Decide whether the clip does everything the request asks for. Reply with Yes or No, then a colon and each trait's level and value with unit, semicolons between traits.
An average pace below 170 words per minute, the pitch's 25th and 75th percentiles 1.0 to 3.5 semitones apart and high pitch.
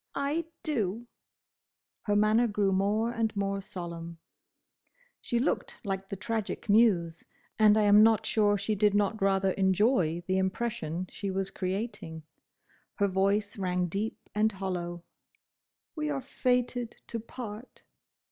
Yes: slow, 135 wpm; average, 2.8 semitones; high, 205 Hz